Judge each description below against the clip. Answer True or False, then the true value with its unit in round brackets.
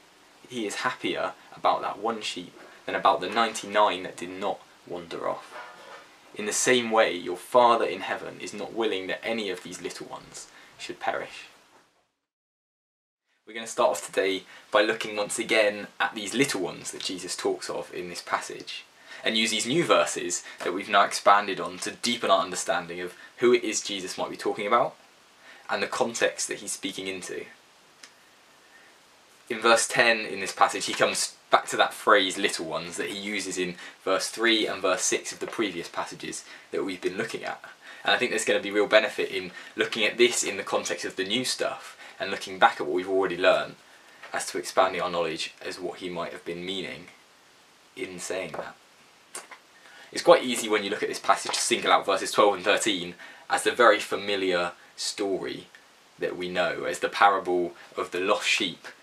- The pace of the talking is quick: False (195 wpm)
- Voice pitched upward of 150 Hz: False (105 Hz)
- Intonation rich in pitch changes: True (5.8 semitones)